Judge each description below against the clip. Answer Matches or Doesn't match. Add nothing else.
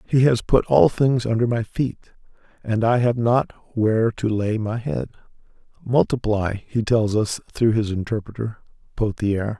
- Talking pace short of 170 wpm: Matches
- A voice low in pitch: Matches